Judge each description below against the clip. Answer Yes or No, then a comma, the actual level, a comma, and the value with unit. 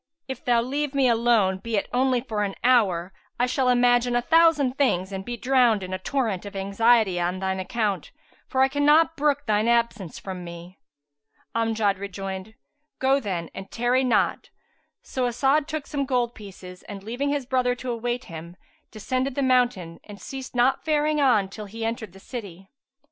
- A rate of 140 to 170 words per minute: No, average, 180 wpm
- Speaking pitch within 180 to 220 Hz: No, high, 235 Hz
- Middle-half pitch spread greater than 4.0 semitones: Yes, average, 5.0 semitones